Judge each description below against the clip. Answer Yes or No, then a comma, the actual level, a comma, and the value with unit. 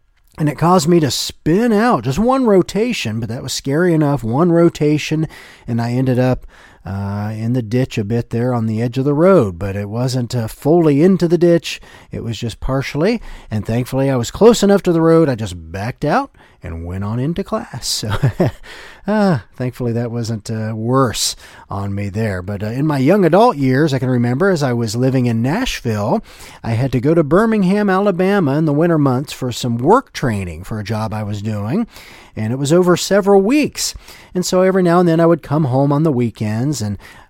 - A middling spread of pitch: No, wide, 7.1 semitones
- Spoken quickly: Yes, fast, 210 wpm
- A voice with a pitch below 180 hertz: Yes, low, 135 Hz